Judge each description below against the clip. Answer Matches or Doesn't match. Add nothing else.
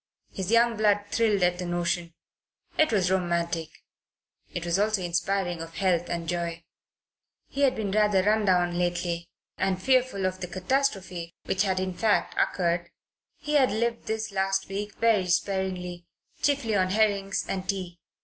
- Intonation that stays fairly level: Doesn't match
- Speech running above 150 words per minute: Matches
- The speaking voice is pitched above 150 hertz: Matches